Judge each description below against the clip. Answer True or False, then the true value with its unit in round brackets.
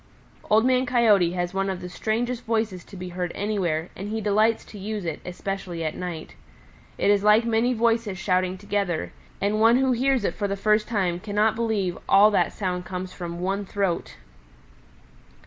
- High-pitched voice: True (200 Hz)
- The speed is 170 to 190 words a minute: True (185 wpm)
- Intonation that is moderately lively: True (3.4 semitones)